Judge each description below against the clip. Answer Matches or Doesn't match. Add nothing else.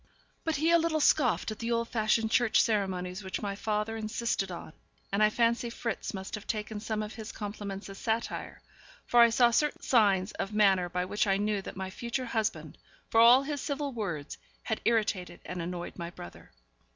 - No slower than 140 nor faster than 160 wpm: Doesn't match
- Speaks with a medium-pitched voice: Doesn't match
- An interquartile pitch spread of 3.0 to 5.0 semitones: Matches